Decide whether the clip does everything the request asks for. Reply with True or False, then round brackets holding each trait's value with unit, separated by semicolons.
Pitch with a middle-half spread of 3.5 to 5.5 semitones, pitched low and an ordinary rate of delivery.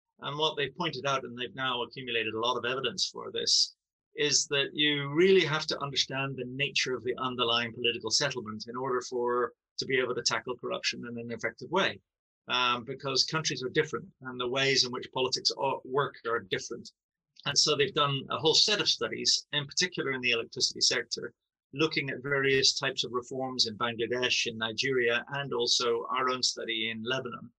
False (3.1 semitones; 130 Hz; 190 wpm)